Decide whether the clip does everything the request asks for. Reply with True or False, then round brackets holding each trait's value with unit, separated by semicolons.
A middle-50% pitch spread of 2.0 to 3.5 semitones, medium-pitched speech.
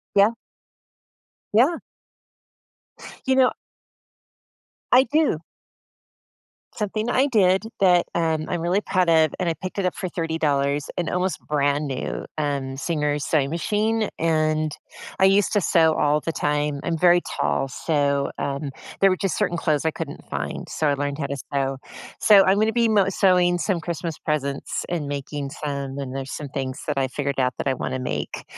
False (4.7 semitones; 160 Hz)